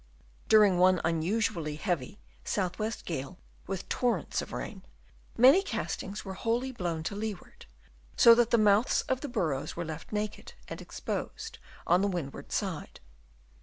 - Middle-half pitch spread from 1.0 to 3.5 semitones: No, average, 5.1 semitones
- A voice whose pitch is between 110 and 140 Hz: No, high, 200 Hz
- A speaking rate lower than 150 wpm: No, average, 155 wpm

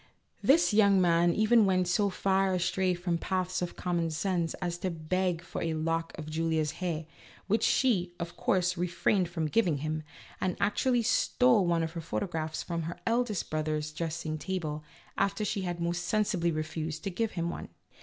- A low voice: No, medium, 175 Hz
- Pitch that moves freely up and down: No, average, 2.8 semitones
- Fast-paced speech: No, average, 180 wpm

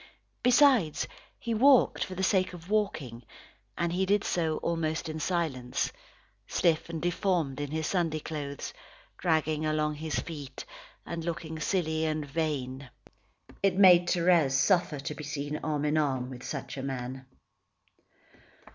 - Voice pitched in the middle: Yes, medium, 160 Hz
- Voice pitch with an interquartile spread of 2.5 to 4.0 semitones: Yes, average, 3.3 semitones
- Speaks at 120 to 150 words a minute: Yes, average, 145 wpm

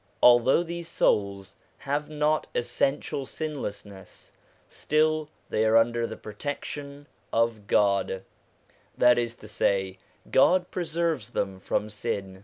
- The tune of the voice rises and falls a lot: Yes, wide, 6.5 semitones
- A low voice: Yes, low, 120 Hz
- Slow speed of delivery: Yes, slow, 120 wpm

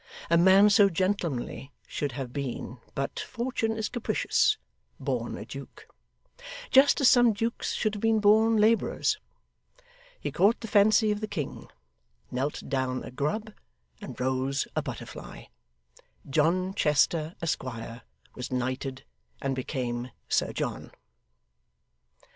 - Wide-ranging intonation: Yes, wide, 8.5 semitones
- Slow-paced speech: Yes, slow, 125 wpm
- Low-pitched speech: No, medium, 170 Hz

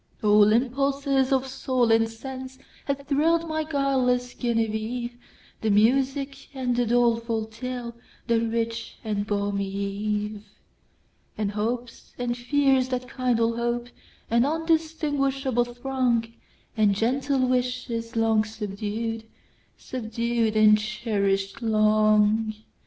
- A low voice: No, high, 235 Hz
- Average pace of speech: No, slow, 90 wpm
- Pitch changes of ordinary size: Yes, average, 3.2 semitones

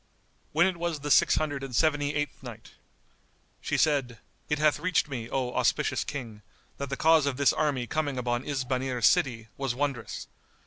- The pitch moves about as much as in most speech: Yes, average, 3.2 semitones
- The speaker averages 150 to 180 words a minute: Yes, average, 175 wpm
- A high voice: No, medium, 140 Hz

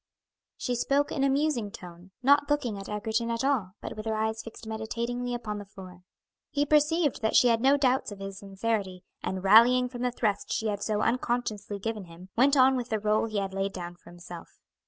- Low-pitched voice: No, high, 220 Hz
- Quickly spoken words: Yes, fast, 215 wpm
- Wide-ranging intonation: No, average, 4.1 semitones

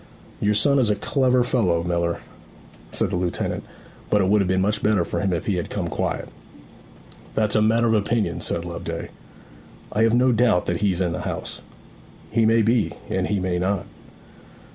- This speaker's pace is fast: No, average, 190 wpm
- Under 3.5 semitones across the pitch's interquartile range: No, average, 4.1 semitones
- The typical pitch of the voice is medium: No, low, 105 Hz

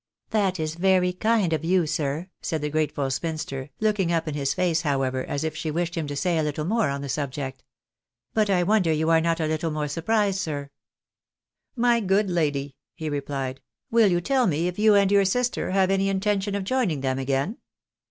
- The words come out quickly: Yes, fast, 215 wpm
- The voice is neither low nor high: Yes, medium, 165 Hz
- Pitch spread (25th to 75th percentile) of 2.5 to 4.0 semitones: No, average, 5.0 semitones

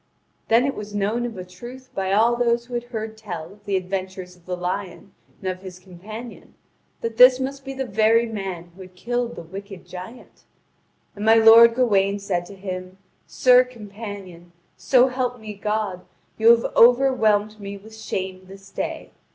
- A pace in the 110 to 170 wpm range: No, average, 180 wpm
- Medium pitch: No, high, 210 Hz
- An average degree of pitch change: Yes, average, 3.9 semitones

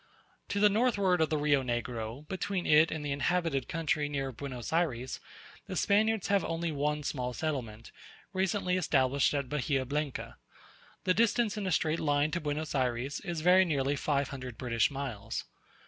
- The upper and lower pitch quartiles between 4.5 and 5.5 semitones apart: Yes, average, 4.9 semitones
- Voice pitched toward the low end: No, medium, 150 Hz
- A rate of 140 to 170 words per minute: Yes, average, 165 wpm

